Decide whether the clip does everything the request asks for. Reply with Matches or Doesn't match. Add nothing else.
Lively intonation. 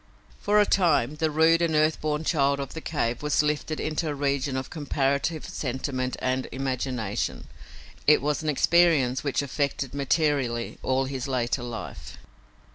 Doesn't match